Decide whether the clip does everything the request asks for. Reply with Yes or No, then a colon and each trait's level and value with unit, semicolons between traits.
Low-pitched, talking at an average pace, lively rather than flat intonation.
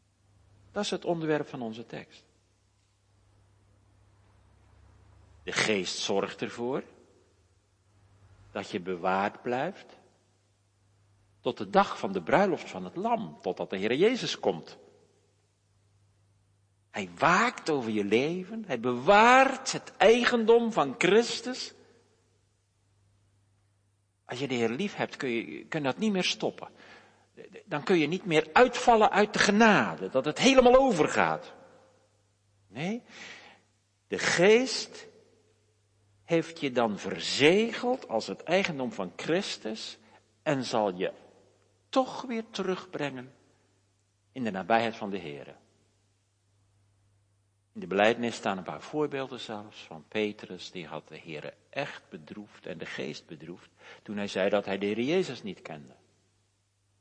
No: low, 105 Hz; slow, 125 wpm; wide, 7.2 semitones